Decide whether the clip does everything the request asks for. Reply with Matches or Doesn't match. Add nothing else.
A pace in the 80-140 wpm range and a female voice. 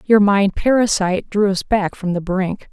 Doesn't match